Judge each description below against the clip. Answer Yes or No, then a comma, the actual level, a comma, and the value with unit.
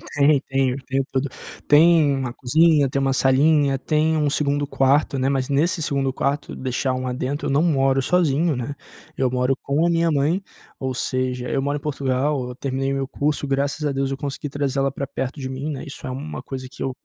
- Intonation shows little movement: Yes, narrow, 1.8 semitones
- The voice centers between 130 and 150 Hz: Yes, medium, 140 Hz